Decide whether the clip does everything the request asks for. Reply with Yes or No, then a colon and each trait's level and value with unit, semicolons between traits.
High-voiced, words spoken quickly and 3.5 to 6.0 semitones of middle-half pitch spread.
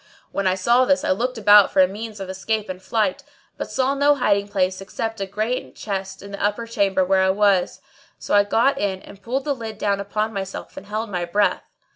No: high, 205 Hz; fast, 230 wpm; average, 2.8 semitones